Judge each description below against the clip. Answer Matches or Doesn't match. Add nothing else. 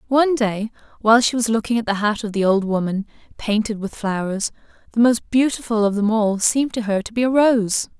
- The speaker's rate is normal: Doesn't match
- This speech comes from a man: Doesn't match